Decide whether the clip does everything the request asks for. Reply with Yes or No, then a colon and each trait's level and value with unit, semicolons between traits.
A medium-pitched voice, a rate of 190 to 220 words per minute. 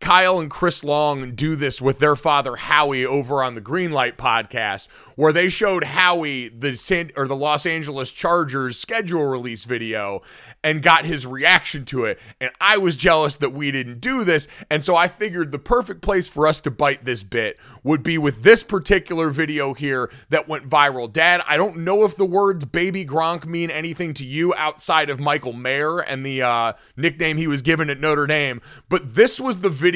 Yes: medium, 155 Hz; average, 200 wpm